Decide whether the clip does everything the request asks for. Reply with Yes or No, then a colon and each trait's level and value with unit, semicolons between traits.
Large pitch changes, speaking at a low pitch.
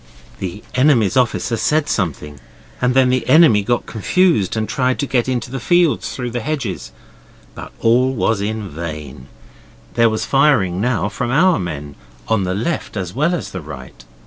Yes: wide, 6.0 semitones; low, 115 Hz